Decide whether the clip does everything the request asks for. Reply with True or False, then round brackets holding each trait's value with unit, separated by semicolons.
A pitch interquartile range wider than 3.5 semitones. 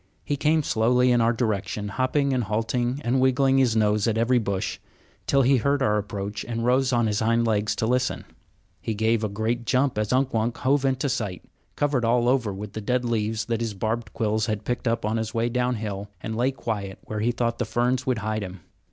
False (2.8 semitones)